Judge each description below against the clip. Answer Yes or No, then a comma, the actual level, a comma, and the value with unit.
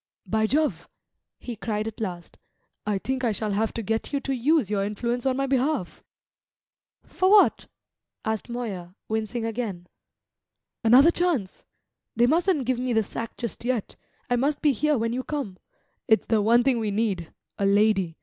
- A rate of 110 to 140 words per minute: No, average, 170 wpm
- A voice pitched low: No, high, 230 Hz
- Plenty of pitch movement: No, average, 3.8 semitones